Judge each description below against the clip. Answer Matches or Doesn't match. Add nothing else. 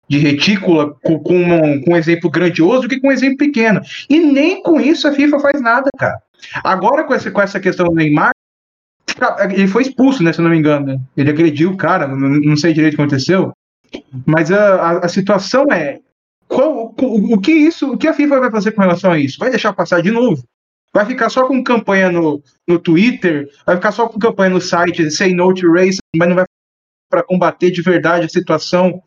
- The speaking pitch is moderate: Matches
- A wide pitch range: Matches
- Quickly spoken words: Matches